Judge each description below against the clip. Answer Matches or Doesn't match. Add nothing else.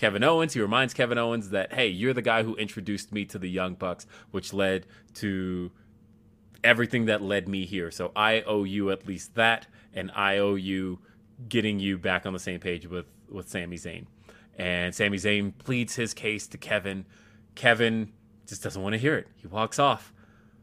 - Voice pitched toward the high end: Doesn't match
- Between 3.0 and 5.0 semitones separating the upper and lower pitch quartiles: Doesn't match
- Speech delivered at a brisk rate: Doesn't match